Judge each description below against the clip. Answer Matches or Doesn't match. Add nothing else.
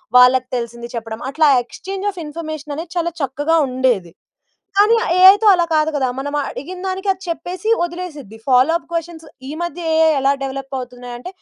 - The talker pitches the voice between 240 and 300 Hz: Doesn't match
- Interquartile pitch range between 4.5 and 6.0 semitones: Matches